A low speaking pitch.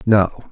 Yes: low, 100 Hz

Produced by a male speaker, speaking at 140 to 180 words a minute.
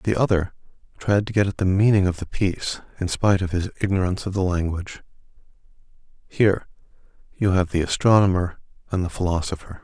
Yes: male; average, 165 wpm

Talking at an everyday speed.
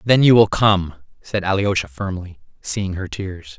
Yes: average, 170 wpm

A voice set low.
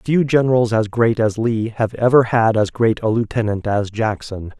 Yes: low, 115 Hz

